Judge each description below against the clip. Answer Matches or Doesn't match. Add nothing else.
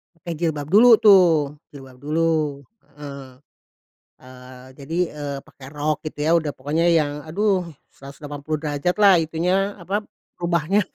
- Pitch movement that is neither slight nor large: Matches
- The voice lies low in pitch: Doesn't match